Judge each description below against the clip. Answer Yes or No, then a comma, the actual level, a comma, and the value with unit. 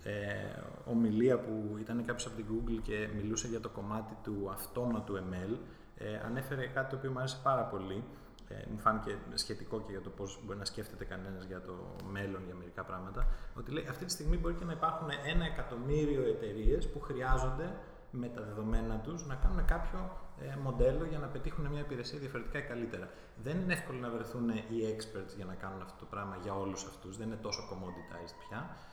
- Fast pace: Yes, fast, 195 wpm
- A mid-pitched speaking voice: No, low, 115 Hz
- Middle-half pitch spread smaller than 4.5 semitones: No, average, 5.1 semitones